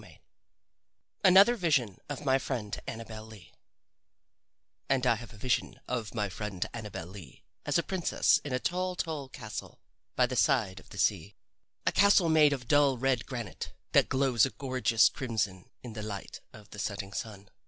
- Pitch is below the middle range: Yes, low, 120 Hz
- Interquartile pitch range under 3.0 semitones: No, average, 4.6 semitones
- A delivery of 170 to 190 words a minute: Yes, average, 175 wpm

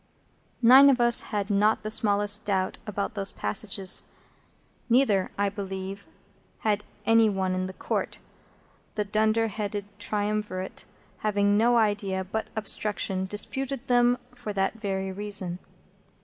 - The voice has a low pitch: No, high, 205 Hz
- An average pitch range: No, narrow, 2.1 semitones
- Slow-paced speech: Yes, slow, 130 wpm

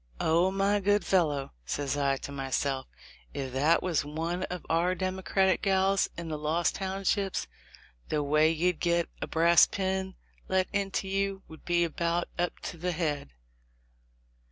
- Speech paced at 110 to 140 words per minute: No, average, 155 wpm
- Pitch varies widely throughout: No, average, 3.7 semitones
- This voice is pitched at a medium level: Yes, medium, 170 Hz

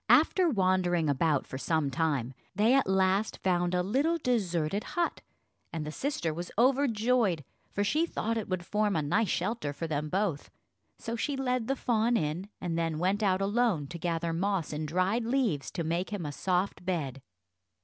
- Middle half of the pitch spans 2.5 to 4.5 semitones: No, wide, 5.5 semitones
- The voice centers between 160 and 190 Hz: Yes, medium, 185 Hz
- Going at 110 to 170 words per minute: No, average, 180 wpm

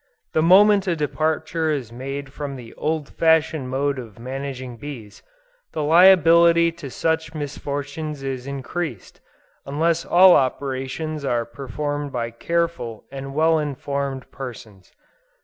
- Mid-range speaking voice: Yes, medium, 145 Hz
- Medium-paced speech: No, slow, 125 wpm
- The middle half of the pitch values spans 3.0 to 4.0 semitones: Yes, average, 3.5 semitones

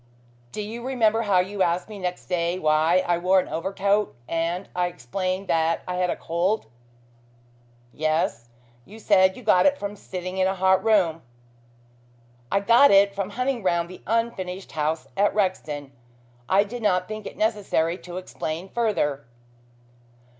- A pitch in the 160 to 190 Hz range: Yes, medium, 185 Hz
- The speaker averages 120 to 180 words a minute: Yes, average, 160 wpm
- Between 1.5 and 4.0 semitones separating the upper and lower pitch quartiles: Yes, average, 3.4 semitones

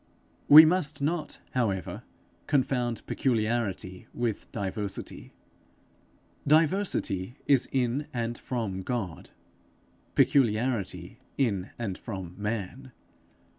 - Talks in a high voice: No, low, 120 Hz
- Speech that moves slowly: Yes, slow, 85 wpm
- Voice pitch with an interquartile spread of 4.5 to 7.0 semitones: Yes, average, 5.3 semitones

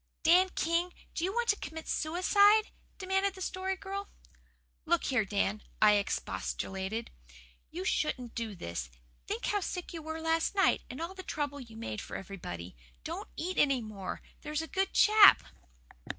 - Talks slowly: No, average, 165 wpm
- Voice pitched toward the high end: Yes, very high, 315 Hz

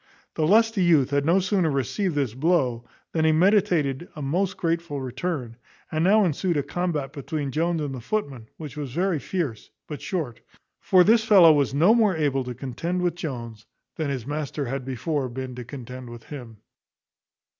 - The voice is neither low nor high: Yes, medium, 150 Hz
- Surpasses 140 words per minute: Yes, average, 180 wpm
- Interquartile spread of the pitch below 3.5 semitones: No, average, 4.9 semitones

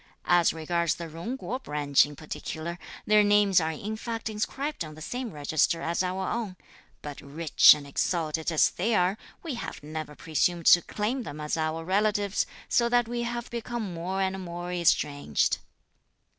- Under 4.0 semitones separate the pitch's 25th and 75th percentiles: No, wide, 5.4 semitones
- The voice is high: No, medium, 175 Hz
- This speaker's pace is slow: No, average, 170 wpm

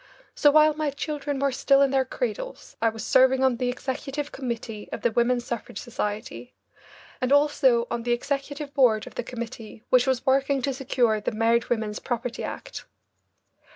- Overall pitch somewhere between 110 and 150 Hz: No, very high, 255 Hz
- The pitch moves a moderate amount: Yes, average, 3.0 semitones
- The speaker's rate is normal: Yes, average, 175 wpm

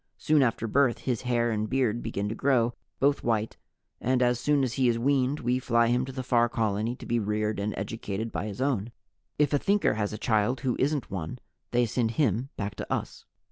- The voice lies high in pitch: No, low, 120 Hz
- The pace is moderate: No, fast, 215 wpm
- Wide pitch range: No, average, 3.2 semitones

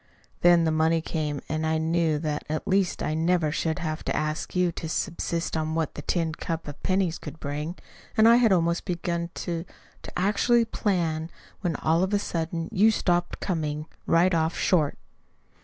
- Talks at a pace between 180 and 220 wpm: Yes, average, 185 wpm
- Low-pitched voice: No, medium, 165 Hz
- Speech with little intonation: Yes, narrow, 2.2 semitones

